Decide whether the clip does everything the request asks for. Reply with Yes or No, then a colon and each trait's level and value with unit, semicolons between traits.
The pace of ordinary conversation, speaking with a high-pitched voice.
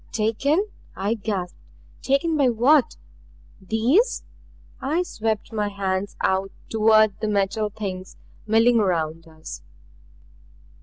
No: slow, 105 wpm; high, 215 Hz